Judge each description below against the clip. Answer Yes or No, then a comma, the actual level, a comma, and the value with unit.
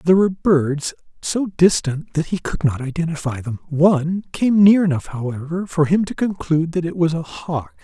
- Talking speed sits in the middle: Yes, average, 190 wpm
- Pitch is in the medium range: Yes, medium, 165 Hz